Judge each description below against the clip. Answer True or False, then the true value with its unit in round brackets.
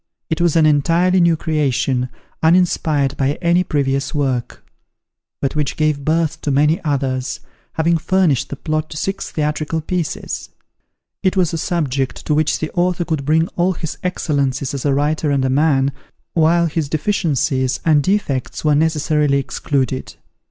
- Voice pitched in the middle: True (155 Hz)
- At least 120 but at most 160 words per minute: True (155 wpm)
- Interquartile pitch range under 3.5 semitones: True (3.1 semitones)